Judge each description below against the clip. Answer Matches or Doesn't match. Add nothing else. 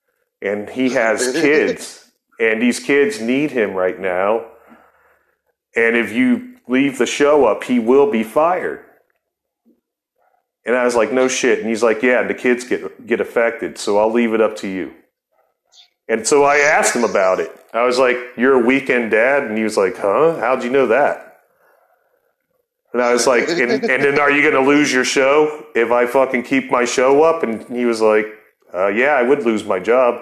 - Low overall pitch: Matches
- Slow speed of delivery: Doesn't match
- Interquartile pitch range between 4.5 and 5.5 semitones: Doesn't match